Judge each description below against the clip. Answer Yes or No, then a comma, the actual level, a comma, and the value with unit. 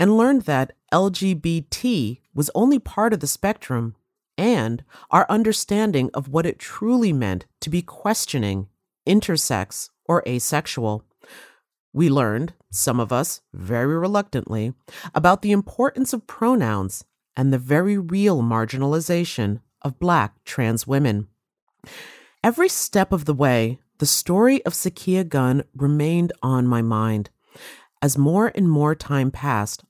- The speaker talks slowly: Yes, slow, 130 wpm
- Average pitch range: No, wide, 7.7 semitones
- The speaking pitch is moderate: Yes, medium, 145 Hz